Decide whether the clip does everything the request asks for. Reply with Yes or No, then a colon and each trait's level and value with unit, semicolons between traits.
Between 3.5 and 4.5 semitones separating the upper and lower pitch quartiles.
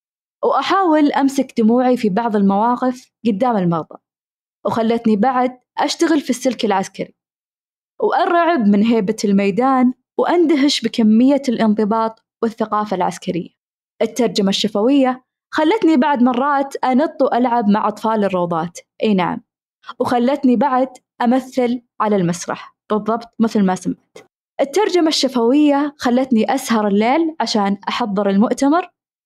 Yes: average, 3.9 semitones